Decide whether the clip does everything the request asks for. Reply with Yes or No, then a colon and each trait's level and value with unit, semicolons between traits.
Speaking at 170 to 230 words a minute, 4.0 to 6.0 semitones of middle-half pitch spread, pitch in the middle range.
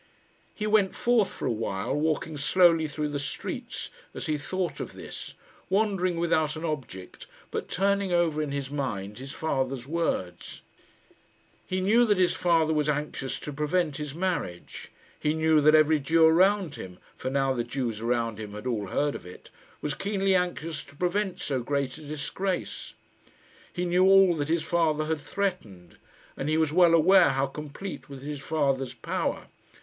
Yes: average, 175 wpm; average, 4.6 semitones; medium, 155 Hz